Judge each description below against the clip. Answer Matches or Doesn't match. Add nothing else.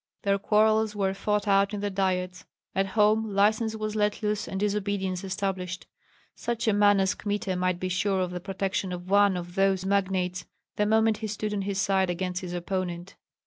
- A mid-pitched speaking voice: Doesn't match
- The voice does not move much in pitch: Matches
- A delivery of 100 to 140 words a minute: Doesn't match